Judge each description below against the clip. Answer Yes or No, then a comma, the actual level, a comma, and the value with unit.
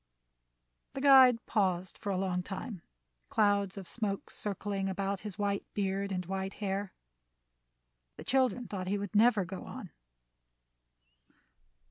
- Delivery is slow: Yes, slow, 130 wpm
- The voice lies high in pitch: Yes, high, 200 Hz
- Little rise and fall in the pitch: Yes, narrow, 1.8 semitones